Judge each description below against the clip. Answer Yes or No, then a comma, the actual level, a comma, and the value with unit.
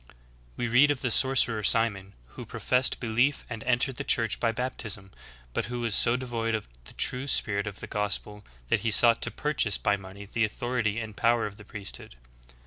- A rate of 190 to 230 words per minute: Yes, average, 200 wpm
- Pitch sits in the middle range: No, low, 115 Hz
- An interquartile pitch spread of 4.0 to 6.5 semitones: No, average, 3.0 semitones